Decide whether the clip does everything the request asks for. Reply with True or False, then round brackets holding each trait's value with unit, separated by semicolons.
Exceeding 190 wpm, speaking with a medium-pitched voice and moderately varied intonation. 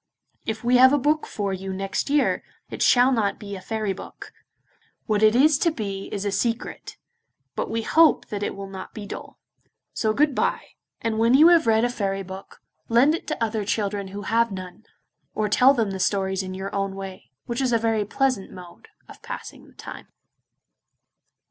False (200 wpm; 215 Hz; 3.9 semitones)